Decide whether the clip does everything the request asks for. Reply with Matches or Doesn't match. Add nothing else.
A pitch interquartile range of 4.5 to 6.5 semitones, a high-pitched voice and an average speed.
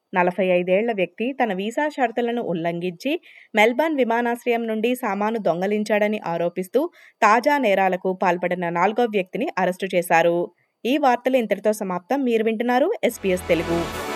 Matches